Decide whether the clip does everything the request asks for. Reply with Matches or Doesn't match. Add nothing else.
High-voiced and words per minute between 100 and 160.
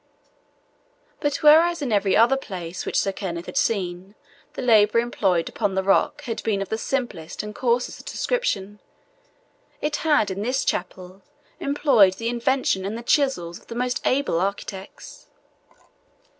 Matches